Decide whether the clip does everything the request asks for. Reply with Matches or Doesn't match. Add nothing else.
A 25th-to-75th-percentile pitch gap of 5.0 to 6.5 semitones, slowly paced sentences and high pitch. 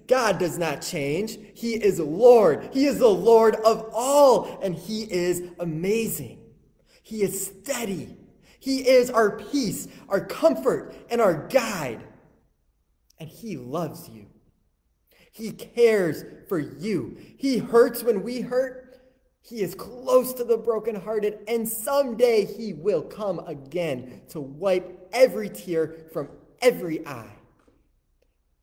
Matches